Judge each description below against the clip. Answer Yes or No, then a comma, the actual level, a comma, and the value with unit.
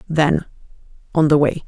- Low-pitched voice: No, medium, 155 Hz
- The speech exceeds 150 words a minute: No, average, 145 wpm